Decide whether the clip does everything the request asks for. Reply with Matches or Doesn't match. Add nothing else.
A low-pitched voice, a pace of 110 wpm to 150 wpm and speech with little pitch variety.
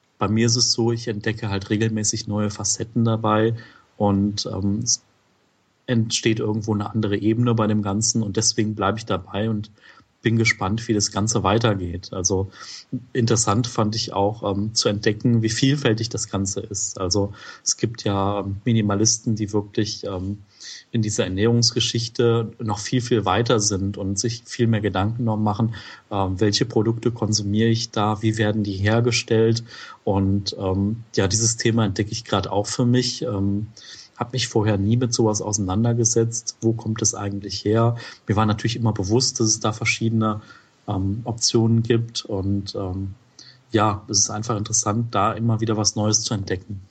Doesn't match